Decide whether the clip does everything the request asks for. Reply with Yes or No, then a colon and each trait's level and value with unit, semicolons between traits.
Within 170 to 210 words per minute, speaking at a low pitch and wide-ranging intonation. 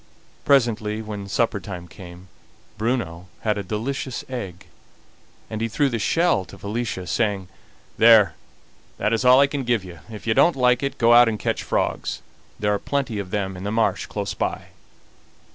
No: average, 180 wpm; low, 110 Hz; average, 3.5 semitones